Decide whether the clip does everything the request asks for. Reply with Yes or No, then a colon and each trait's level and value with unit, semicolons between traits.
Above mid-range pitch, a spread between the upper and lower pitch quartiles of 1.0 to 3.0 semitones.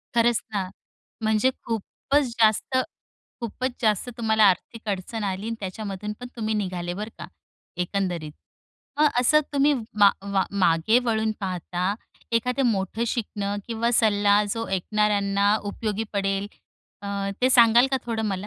Yes: high, 210 Hz; average, 2.7 semitones